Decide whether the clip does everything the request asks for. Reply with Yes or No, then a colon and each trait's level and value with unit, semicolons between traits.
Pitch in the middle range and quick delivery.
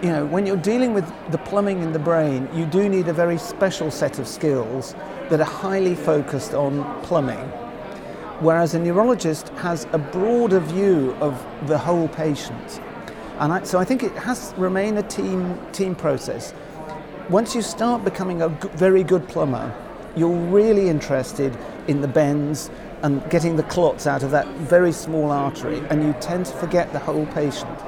No: medium, 165 Hz; average, 180 wpm